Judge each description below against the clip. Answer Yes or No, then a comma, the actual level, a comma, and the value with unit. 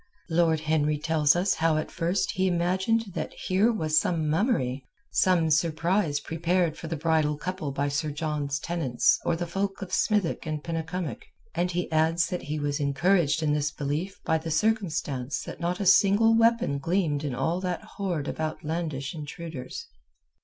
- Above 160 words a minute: Yes, average, 170 wpm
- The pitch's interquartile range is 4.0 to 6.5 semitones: No, average, 3.2 semitones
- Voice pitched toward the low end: No, medium, 165 Hz